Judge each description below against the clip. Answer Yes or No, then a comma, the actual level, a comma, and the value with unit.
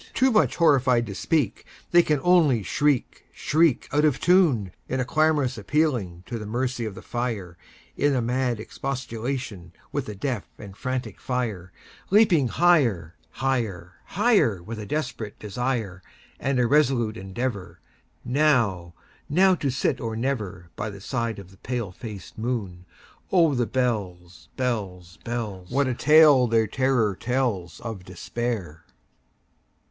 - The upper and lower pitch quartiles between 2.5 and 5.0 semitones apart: No, wide, 5.5 semitones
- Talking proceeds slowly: Yes, slow, 120 wpm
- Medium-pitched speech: No, low, 120 Hz